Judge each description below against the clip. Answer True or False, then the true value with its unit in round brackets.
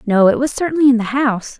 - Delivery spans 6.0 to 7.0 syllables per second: True (6.8 syllables/s)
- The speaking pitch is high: True (245 Hz)